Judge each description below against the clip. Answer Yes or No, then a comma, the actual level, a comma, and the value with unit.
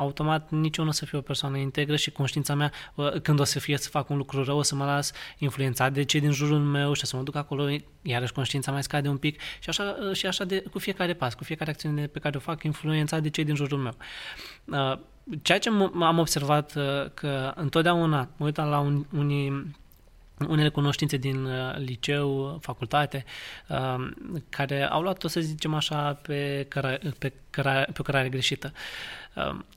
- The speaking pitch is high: No, medium, 145 Hz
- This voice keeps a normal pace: No, fast, 180 wpm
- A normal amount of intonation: No, narrow, 1.9 semitones